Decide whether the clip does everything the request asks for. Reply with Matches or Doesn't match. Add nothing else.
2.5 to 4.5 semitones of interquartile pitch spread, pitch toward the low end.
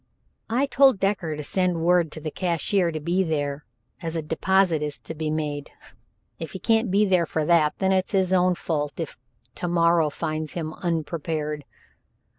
Doesn't match